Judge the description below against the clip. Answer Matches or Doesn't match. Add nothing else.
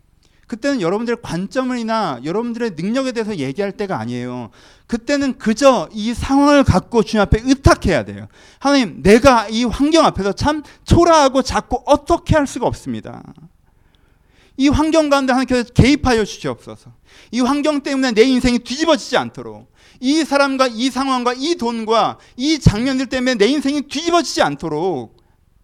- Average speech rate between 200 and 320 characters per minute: Doesn't match